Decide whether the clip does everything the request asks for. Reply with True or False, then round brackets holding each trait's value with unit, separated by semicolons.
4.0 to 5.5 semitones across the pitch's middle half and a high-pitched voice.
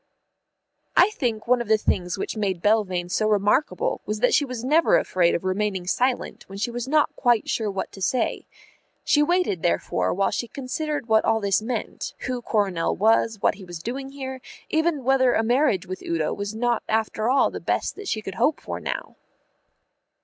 True (4.9 semitones; 220 Hz)